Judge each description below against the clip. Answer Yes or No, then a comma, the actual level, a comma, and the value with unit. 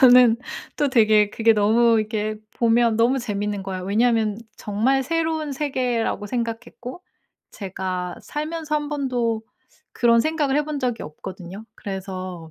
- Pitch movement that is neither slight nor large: Yes, average, 4.4 semitones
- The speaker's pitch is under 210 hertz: No, high, 230 Hz